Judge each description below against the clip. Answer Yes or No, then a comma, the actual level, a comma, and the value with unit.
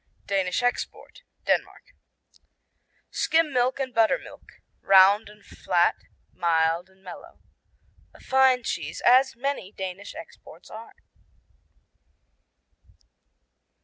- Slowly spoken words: Yes, slow, 90 wpm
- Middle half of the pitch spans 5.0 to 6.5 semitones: Yes, wide, 5.5 semitones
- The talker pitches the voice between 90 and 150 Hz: No, high, 210 Hz